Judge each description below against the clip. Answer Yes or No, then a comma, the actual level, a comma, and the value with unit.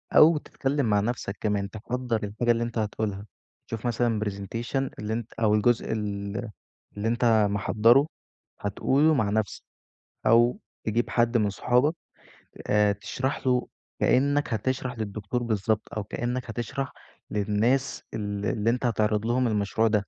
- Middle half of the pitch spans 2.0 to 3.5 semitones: Yes, average, 2.9 semitones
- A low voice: Yes, low, 115 Hz